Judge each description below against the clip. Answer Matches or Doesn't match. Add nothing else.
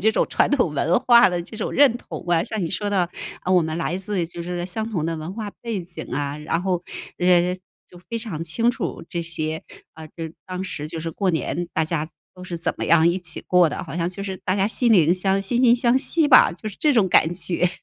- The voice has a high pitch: Doesn't match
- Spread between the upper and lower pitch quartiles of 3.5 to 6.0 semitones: Matches